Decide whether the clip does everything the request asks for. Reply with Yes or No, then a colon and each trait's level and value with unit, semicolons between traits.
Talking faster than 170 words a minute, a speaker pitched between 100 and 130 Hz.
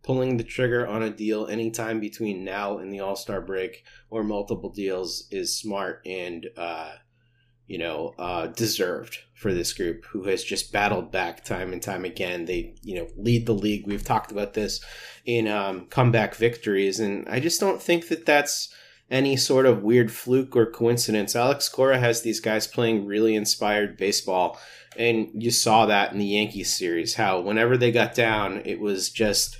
Yes: average, 180 wpm; low, 110 Hz